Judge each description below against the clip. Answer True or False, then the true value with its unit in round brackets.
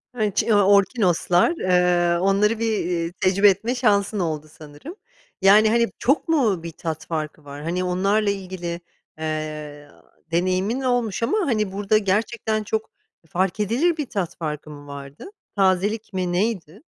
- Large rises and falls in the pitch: False (4.2 semitones)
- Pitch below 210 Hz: True (190 Hz)